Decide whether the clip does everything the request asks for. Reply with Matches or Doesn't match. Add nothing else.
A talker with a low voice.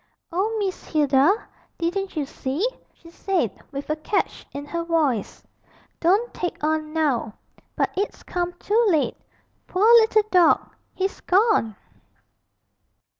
Doesn't match